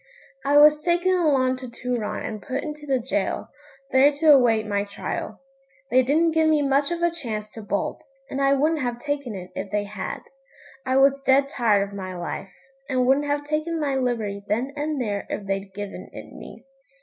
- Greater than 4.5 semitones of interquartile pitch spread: Yes, wide, 5.6 semitones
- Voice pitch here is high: Yes, very high, 260 Hz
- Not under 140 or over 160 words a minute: No, average, 195 wpm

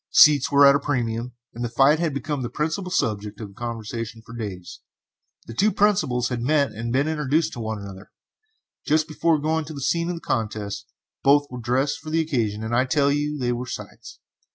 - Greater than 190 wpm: Yes, fast, 205 wpm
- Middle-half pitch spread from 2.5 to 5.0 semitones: Yes, average, 4.7 semitones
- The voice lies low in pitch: Yes, low, 130 Hz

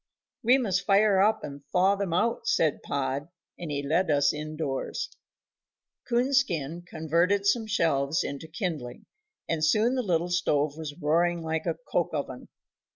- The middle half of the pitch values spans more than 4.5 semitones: Yes, average, 5.1 semitones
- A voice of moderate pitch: Yes, medium, 165 Hz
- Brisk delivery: No, average, 155 wpm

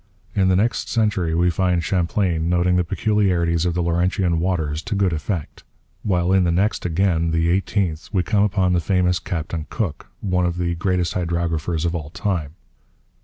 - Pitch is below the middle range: Yes, very low, 90 Hz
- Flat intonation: Yes, narrow, 2.2 semitones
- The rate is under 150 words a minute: No, average, 175 wpm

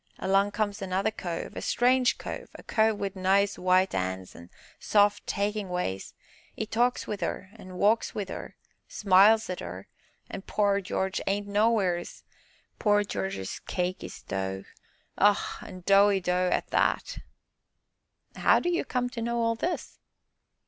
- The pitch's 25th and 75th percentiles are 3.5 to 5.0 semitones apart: No, narrow, 2.6 semitones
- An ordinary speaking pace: Yes, average, 150 wpm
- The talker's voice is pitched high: Yes, high, 200 Hz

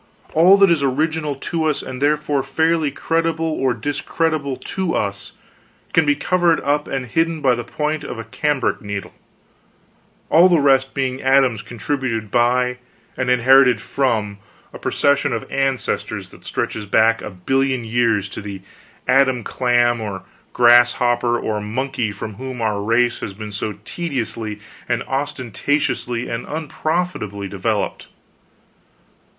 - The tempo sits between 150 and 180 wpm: No, average, 140 wpm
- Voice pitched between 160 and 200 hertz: No, low, 130 Hz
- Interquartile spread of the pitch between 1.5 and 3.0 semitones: No, average, 4.4 semitones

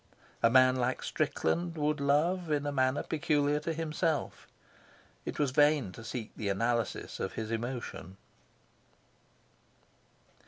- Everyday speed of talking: No, slow, 125 wpm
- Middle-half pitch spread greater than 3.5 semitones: Yes, average, 4.1 semitones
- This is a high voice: No, medium, 140 Hz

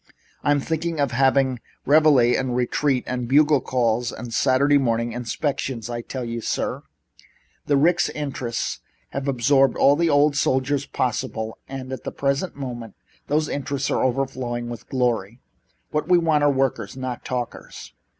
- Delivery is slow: No, average, 150 wpm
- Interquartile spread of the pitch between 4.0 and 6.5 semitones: No, average, 2.9 semitones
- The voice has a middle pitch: No, low, 130 Hz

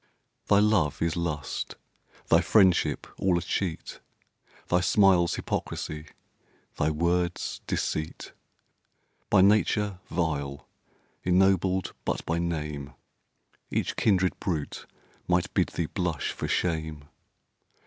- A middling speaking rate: No, slow, 105 wpm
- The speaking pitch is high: No, very low, 85 Hz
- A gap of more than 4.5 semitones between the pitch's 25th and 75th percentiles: No, average, 3.2 semitones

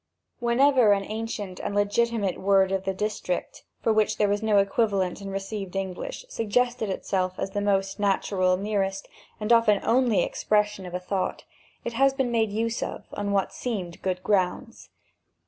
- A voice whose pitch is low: No, high, 205 Hz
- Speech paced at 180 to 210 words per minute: No, average, 165 wpm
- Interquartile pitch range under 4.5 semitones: Yes, average, 2.7 semitones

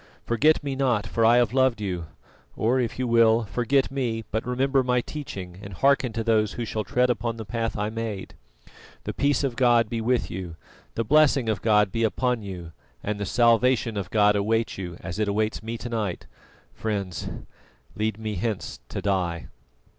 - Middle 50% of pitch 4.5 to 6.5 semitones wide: No, average, 3.1 semitones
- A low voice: Yes, low, 115 Hz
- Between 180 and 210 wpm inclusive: Yes, average, 190 wpm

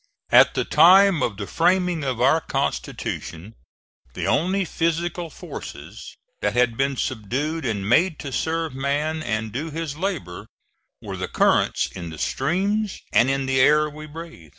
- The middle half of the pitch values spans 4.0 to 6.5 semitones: Yes, average, 5.1 semitones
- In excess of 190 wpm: No, average, 155 wpm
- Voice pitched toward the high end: No, medium, 150 Hz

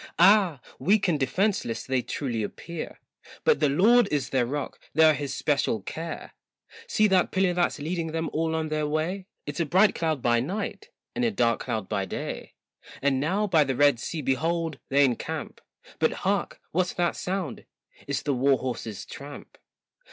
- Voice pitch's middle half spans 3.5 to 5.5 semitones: Yes, average, 5.1 semitones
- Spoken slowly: No, average, 175 wpm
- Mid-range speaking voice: Yes, medium, 155 Hz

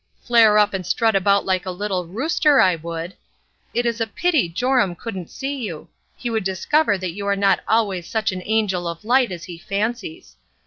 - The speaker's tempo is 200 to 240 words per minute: Yes, fast, 205 wpm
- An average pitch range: Yes, average, 4.4 semitones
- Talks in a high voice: Yes, high, 205 Hz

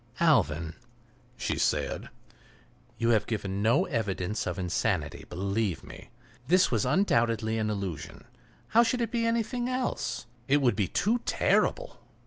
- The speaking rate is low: Yes, slow, 130 wpm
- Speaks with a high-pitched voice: No, low, 115 Hz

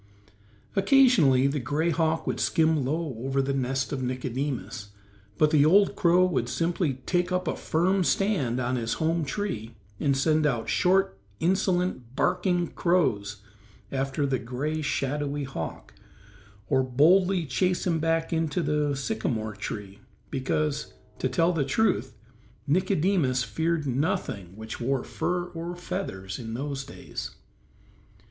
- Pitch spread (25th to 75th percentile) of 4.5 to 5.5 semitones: Yes, average, 5.2 semitones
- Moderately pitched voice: Yes, medium, 150 Hz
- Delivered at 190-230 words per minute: No, slow, 135 wpm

